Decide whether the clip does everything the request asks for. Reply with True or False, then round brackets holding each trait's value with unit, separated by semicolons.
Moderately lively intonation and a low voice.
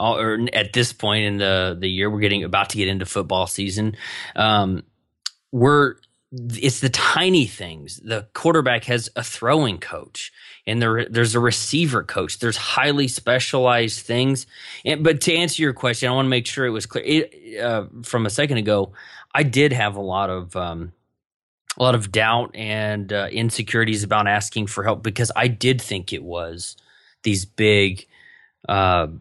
True (3.7 semitones; 115 Hz)